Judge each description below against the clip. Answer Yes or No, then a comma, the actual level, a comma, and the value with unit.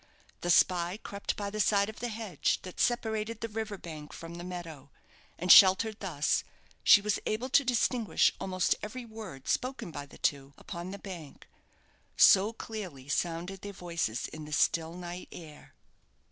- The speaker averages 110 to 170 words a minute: Yes, average, 165 wpm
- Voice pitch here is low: No, medium, 185 Hz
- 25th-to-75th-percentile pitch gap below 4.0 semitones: No, average, 4.5 semitones